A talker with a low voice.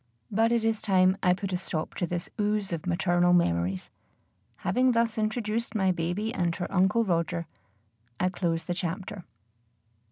No: medium, 185 Hz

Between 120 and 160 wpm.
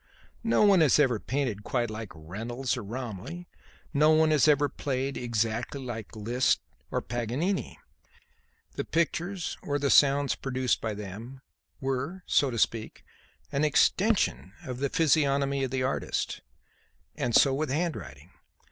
Yes: average, 140 wpm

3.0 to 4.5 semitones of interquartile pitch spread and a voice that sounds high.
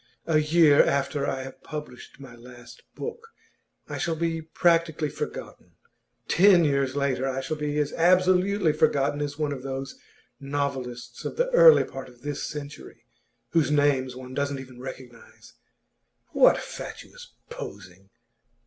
No: average, 3.4 semitones; medium, 145 Hz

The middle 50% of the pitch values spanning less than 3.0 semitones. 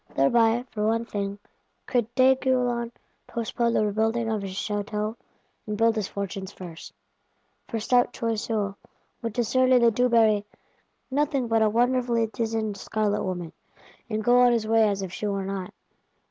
Yes: narrow, 2.5 semitones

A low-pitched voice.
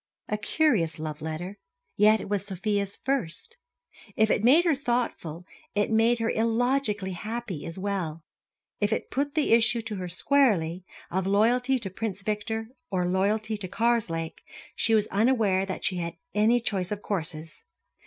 No: high, 210 Hz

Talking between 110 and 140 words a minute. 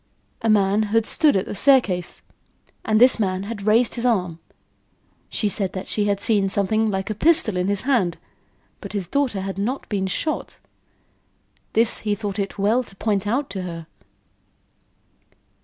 No: average, 170 wpm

